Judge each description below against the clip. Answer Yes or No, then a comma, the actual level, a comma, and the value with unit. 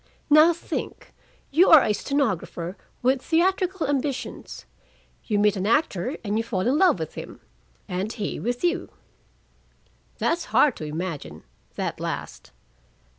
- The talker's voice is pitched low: No, high, 245 Hz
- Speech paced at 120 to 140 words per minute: Yes, slow, 135 wpm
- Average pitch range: No, wide, 8.2 semitones